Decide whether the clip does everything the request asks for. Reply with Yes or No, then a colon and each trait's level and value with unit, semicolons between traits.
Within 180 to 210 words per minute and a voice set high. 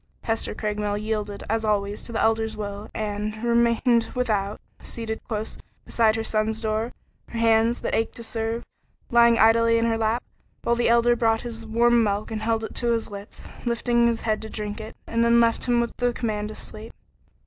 Yes: average, 200 wpm; high, 225 Hz